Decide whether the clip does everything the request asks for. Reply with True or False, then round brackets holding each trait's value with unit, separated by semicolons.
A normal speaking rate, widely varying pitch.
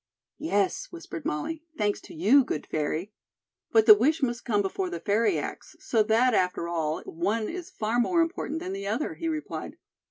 True (185 wpm; 7.8 semitones)